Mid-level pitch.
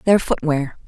Yes: medium, 160 Hz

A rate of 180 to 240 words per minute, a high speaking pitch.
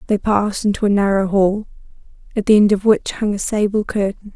Yes: fast, 205 wpm; high, 205 Hz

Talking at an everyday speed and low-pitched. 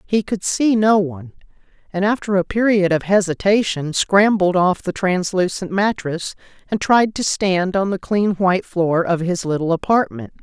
No: average, 165 wpm; medium, 185 Hz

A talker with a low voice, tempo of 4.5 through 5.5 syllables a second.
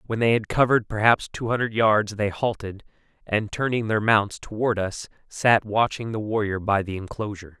Yes: low, 105 Hz; 5.1 syllables/s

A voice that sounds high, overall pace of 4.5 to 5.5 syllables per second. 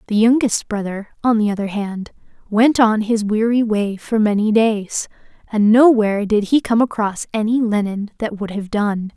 Yes: high, 215 Hz; 4.7 syllables/s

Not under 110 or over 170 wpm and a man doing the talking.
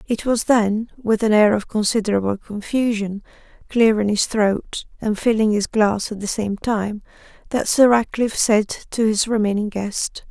No: average, 165 wpm; female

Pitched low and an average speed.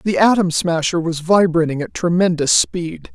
No: medium, 170 Hz; average, 155 wpm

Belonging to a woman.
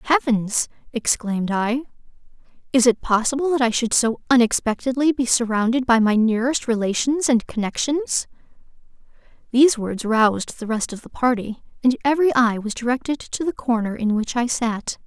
Yes: female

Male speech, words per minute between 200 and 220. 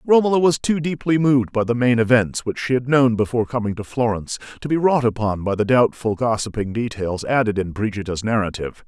Yes: male; fast, 205 wpm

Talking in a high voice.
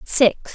Yes: high, 235 Hz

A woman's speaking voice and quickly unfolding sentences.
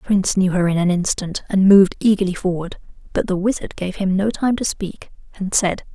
Yes: female; fast, 220 wpm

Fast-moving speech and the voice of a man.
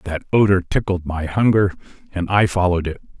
No: average, 170 wpm; male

